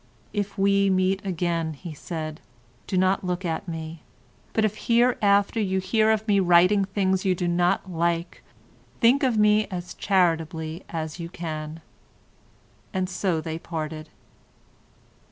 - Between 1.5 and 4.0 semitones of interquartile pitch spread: Yes, average, 3.3 semitones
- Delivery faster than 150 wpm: No, average, 140 wpm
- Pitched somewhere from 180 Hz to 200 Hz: Yes, medium, 185 Hz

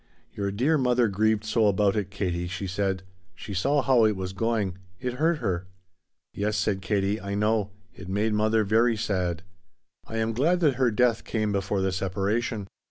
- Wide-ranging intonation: No, average, 2.9 semitones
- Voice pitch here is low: Yes, low, 105 Hz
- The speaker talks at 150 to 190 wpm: Yes, average, 180 wpm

